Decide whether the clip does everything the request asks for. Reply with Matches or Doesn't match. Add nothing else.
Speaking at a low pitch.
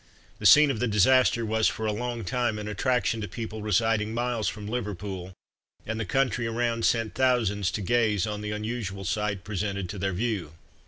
Matches